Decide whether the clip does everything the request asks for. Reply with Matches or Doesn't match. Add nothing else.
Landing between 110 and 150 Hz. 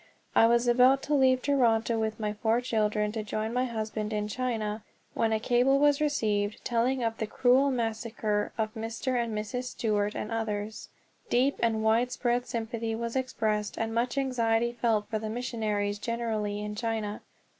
Doesn't match